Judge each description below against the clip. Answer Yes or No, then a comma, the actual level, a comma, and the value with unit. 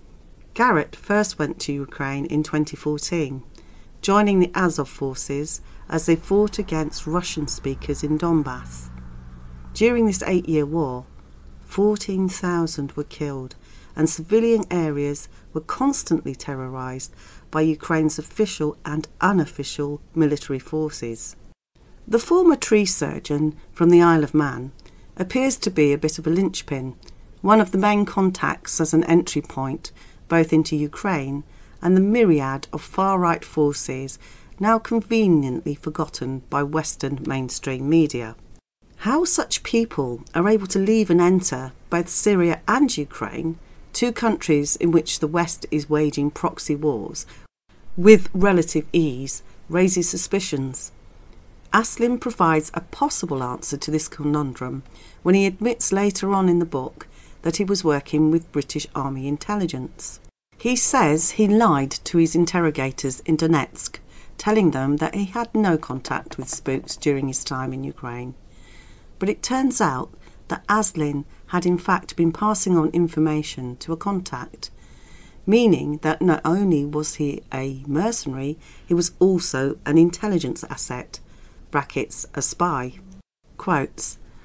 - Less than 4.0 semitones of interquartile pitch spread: No, average, 4.9 semitones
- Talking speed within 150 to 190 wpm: No, slow, 135 wpm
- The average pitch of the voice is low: No, medium, 155 Hz